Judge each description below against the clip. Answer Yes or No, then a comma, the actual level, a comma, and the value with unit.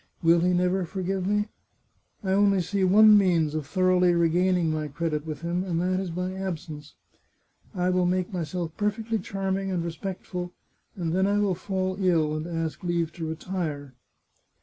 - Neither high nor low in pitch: Yes, medium, 180 Hz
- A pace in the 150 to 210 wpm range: Yes, average, 170 wpm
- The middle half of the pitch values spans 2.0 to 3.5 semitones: Yes, narrow, 2.4 semitones